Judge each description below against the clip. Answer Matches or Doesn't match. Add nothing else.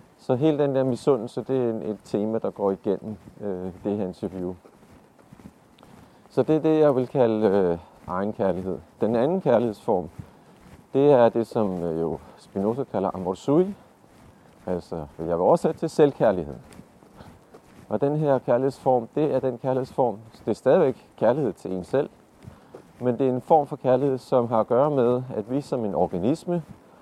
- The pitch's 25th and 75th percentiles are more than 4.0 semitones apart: Matches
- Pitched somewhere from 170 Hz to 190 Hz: Doesn't match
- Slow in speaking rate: Doesn't match